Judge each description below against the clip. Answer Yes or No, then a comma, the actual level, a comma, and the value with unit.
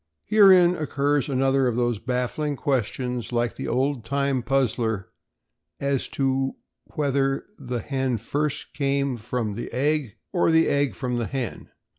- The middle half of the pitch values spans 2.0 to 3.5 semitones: Yes, narrow, 2.5 semitones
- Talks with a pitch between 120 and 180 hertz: Yes, low, 135 Hz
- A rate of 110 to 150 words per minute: Yes, average, 140 wpm